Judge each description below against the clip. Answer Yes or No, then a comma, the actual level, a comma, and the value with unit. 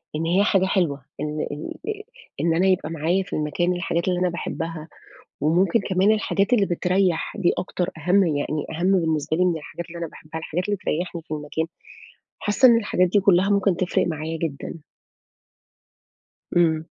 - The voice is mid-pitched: Yes, medium, 175 Hz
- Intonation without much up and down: No, average, 3.0 semitones